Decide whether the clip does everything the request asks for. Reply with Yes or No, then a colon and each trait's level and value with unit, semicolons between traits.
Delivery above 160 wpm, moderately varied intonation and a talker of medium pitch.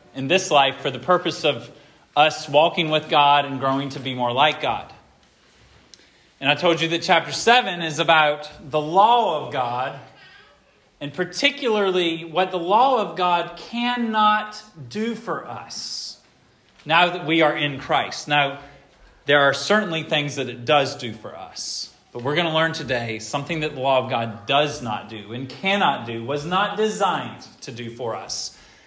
Yes: average, 175 wpm; average, 4.6 semitones; medium, 150 Hz